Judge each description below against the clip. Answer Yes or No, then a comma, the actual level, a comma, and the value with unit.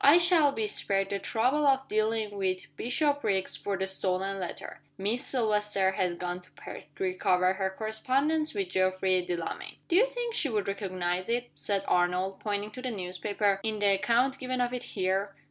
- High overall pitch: Yes, high, 205 Hz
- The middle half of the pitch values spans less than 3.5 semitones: No, average, 4.7 semitones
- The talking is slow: No, average, 180 wpm